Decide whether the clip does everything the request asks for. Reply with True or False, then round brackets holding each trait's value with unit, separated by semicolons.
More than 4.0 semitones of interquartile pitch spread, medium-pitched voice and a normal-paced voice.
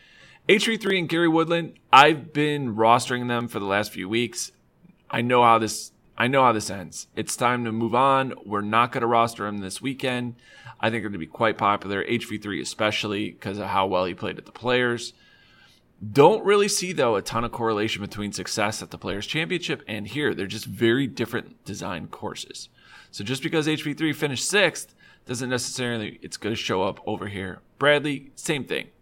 False (4.6 semitones; 120 Hz; 195 wpm)